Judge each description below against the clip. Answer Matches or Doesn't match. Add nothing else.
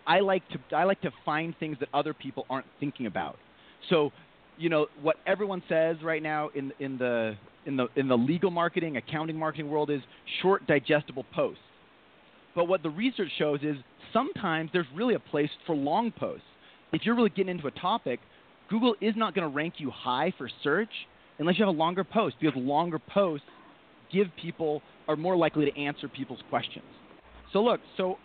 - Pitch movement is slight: Doesn't match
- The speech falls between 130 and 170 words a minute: Doesn't match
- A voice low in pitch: Doesn't match